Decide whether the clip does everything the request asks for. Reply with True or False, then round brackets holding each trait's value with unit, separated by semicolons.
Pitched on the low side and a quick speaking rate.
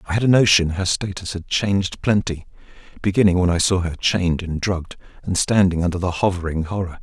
False (90 Hz; 195 wpm)